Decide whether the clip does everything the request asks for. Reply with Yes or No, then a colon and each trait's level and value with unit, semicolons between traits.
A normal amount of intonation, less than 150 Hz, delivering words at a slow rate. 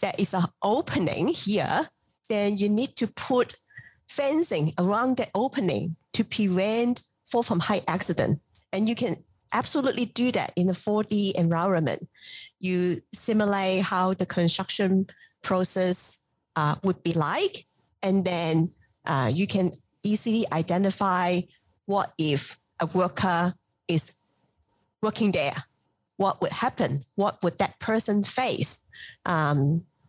No: average, 3.8 semitones; high, 190 Hz; slow, 125 wpm